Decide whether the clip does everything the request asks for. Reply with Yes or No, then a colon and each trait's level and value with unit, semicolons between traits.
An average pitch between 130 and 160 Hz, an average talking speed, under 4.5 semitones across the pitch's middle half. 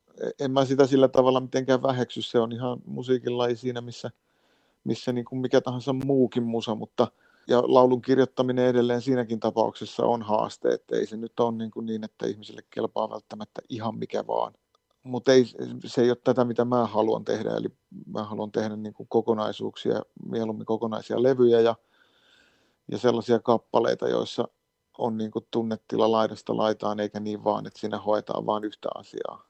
No: low, 120 Hz; average, 170 wpm; narrow, 2.6 semitones